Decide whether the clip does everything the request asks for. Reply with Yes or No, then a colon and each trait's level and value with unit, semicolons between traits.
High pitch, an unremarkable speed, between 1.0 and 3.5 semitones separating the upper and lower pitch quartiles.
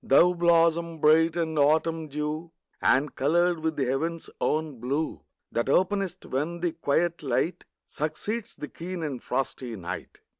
No: medium, 160 Hz; average, 145 wpm; average, 2.9 semitones